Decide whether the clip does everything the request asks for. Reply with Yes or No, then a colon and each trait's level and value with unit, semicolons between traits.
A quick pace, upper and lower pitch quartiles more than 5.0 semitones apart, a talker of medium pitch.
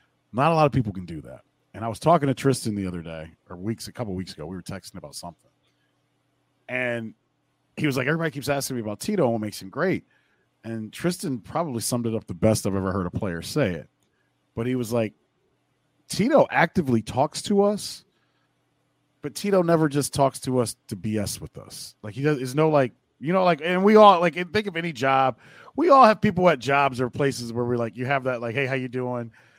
No: fast, 235 wpm; wide, 5.6 semitones; low, 130 Hz